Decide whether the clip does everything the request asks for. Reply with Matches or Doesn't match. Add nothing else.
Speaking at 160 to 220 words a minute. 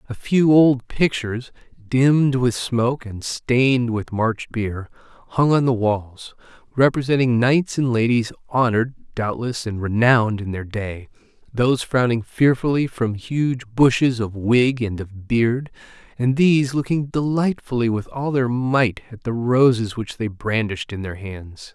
Doesn't match